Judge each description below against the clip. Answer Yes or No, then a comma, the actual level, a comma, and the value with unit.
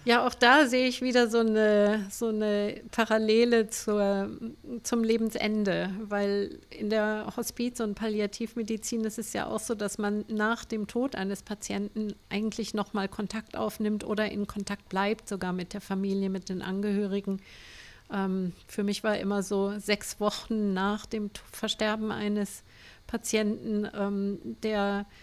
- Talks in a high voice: Yes, high, 210 Hz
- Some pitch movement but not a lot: No, narrow, 1.7 semitones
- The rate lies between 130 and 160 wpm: Yes, average, 150 wpm